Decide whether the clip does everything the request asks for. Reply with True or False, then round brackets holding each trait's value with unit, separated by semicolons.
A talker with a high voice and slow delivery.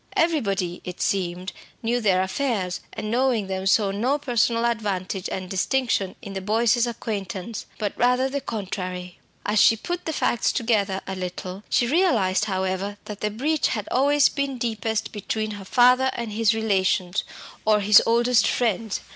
False (215 Hz; 160 wpm)